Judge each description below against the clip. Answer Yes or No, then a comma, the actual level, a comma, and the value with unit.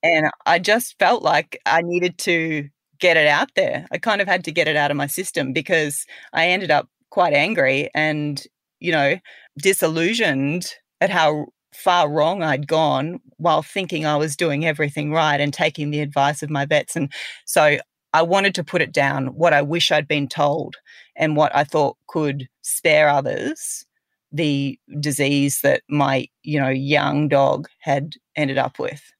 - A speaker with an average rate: Yes, average, 175 wpm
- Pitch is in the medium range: Yes, medium, 150 Hz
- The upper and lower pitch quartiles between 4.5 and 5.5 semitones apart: No, average, 2.8 semitones